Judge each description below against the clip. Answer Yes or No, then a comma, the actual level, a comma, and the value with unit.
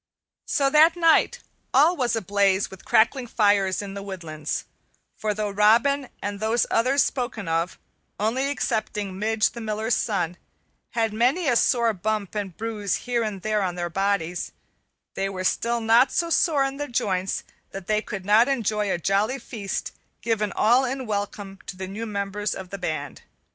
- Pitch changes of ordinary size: Yes, average, 3.4 semitones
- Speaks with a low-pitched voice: No, high, 215 Hz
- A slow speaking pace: No, average, 170 wpm